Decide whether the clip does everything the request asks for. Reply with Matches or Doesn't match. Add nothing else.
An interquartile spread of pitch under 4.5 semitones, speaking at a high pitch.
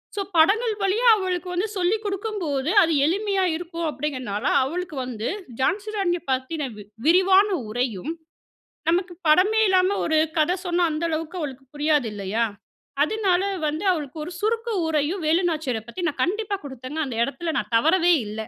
Doesn't match